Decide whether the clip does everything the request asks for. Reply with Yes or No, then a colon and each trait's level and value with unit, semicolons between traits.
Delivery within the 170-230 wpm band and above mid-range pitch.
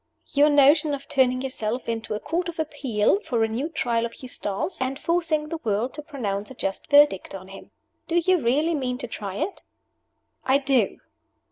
Yes: average, 190 wpm; very high, 265 Hz